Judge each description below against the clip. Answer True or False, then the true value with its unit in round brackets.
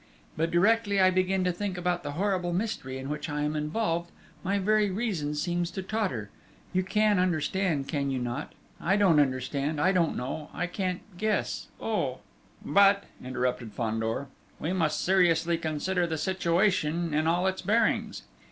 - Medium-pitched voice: True (175 Hz)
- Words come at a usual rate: True (165 wpm)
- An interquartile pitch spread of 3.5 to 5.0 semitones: True (4.2 semitones)